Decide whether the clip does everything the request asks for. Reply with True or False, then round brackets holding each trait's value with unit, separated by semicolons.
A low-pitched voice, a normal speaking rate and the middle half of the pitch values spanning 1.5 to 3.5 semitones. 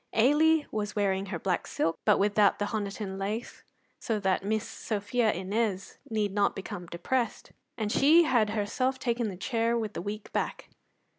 False (210 Hz; 165 wpm; 2.8 semitones)